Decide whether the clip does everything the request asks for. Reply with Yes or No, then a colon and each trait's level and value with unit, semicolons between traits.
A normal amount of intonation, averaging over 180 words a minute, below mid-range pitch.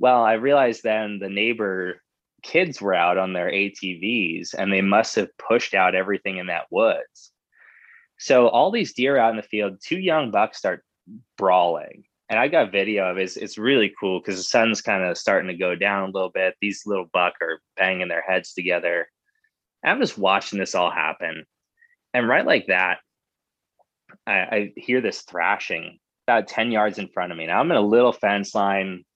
Yes: average, 4.3 semitones; average, 195 wpm; low, 100 Hz